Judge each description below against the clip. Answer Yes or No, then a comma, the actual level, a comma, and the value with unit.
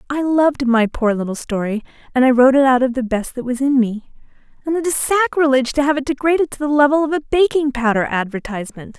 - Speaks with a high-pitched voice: Yes, very high, 265 Hz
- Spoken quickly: Yes, fast, 225 wpm